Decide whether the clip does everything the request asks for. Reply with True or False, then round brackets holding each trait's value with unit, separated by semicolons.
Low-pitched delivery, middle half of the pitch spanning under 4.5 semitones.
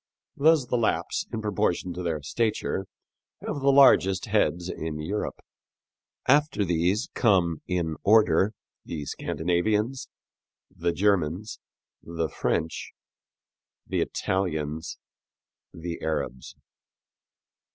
False (90 Hz; 4.8 semitones)